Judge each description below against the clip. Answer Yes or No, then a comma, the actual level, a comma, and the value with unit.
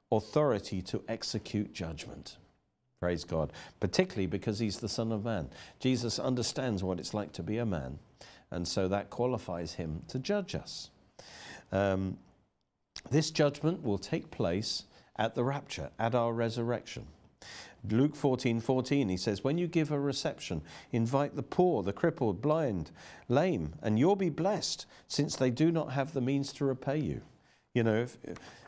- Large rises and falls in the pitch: Yes, wide, 6.4 semitones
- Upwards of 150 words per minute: Yes, average, 160 wpm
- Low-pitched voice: Yes, low, 115 Hz